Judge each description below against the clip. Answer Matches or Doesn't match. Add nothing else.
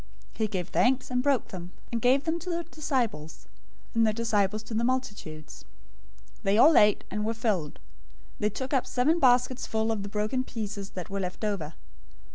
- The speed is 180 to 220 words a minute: Matches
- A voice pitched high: Matches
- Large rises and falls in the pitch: Doesn't match